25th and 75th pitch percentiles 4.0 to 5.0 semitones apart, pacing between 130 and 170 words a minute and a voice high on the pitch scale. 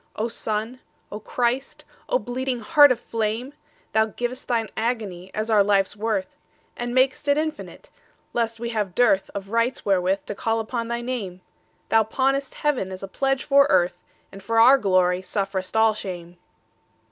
Yes: average, 4.3 semitones; average, 150 wpm; high, 225 Hz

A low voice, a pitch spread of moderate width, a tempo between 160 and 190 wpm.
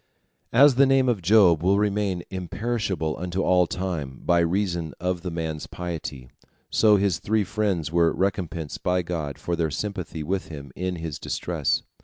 Yes: very low, 90 Hz; average, 3.5 semitones; average, 165 wpm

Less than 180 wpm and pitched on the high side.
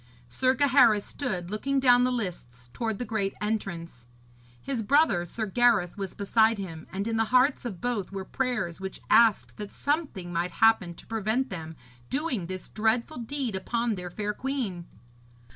Yes: average, 165 wpm; high, 215 Hz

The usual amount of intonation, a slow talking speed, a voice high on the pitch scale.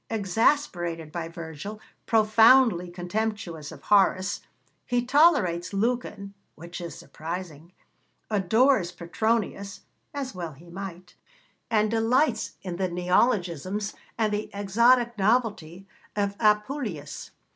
Yes: average, 4.4 semitones; slow, 105 wpm; high, 200 Hz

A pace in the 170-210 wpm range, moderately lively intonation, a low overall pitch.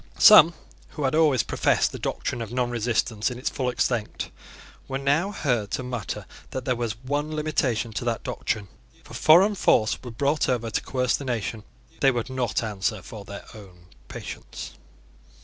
Yes: average, 180 wpm; average, 3.8 semitones; low, 125 Hz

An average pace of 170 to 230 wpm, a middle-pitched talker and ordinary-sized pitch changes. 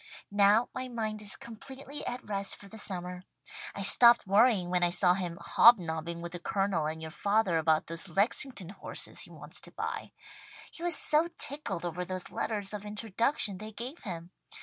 No: average, 180 wpm; high, 200 Hz; average, 4.4 semitones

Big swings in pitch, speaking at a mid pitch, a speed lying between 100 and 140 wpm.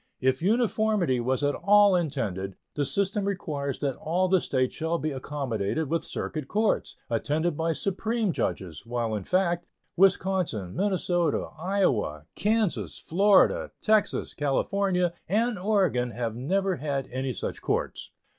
Yes: wide, 7.0 semitones; medium, 165 Hz; slow, 135 wpm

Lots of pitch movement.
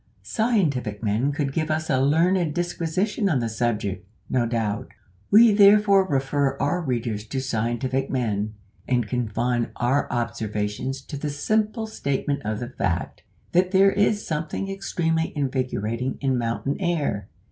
Yes: wide, 6.6 semitones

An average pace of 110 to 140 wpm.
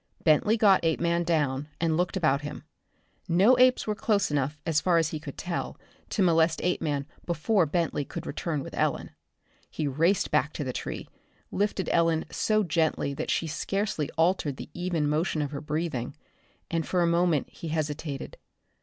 No: average, 170 wpm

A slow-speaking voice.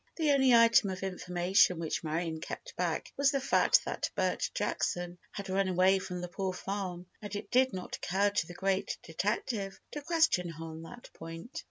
No: average, 190 wpm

